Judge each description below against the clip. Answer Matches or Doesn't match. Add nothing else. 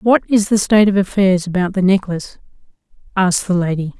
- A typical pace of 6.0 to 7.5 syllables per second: Matches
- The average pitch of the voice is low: Doesn't match